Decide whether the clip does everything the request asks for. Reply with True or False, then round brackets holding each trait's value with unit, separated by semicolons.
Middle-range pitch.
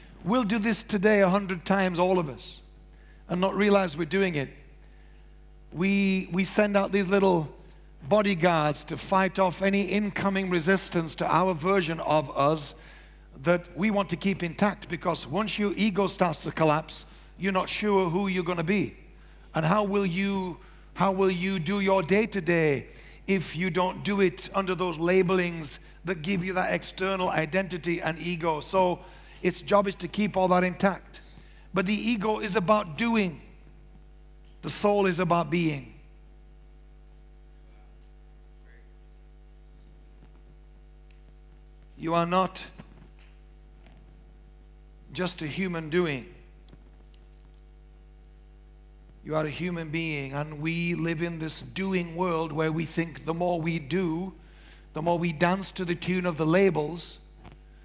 True (180 Hz)